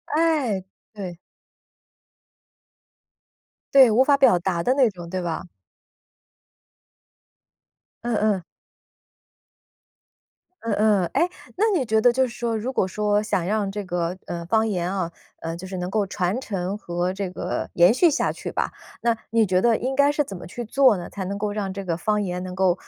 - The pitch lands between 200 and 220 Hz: Yes, high, 205 Hz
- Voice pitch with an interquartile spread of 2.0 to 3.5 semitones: No, average, 4.5 semitones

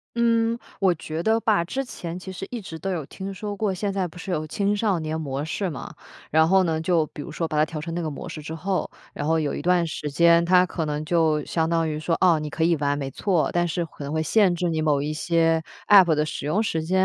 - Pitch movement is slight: No, average, 3.2 semitones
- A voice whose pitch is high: No, medium, 165 Hz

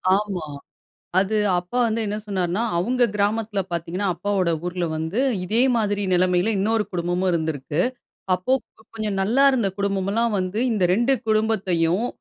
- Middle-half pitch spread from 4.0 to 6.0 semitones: No, average, 3.6 semitones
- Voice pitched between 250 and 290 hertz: No, high, 200 Hz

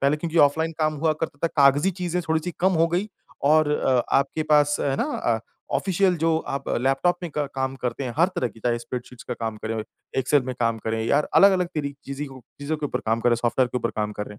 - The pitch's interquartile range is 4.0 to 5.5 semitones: Yes, average, 4.6 semitones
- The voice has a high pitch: No, medium, 140 Hz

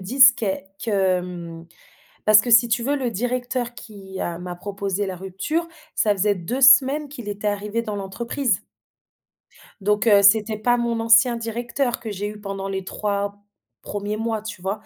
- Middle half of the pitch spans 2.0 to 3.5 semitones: Yes, average, 3.2 semitones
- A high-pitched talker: Yes, high, 210 Hz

